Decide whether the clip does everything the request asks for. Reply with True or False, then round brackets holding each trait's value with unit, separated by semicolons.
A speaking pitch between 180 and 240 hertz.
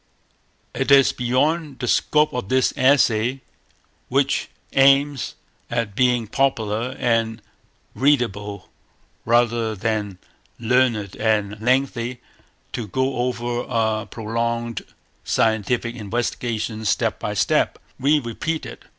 False (120 Hz)